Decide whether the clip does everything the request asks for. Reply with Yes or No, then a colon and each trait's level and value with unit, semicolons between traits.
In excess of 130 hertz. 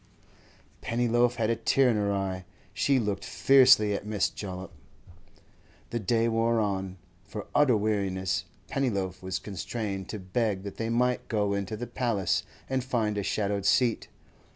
No: low, 105 Hz